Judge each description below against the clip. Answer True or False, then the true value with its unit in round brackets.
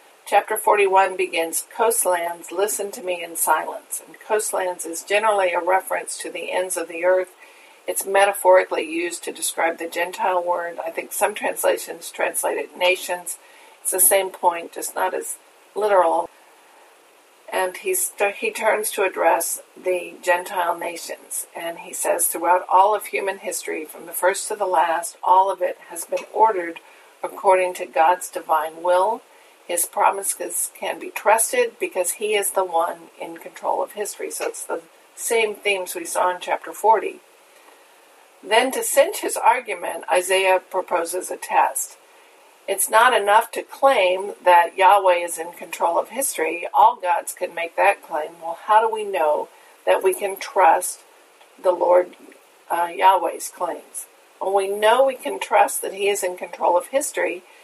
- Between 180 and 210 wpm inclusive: False (165 wpm)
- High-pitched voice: True (195 Hz)